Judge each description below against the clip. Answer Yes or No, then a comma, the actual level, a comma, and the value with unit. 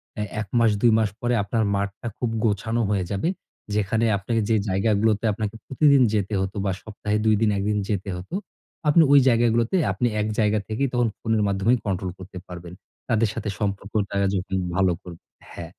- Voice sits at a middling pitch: No, low, 105 Hz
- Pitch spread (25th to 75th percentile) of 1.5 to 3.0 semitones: Yes, narrow, 2.6 semitones